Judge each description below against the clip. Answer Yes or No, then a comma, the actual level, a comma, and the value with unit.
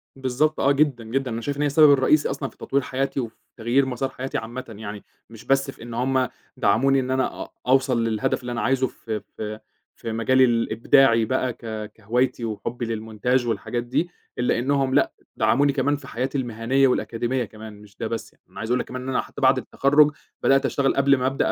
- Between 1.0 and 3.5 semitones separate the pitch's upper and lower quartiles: Yes, average, 2.9 semitones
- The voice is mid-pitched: No, low, 125 Hz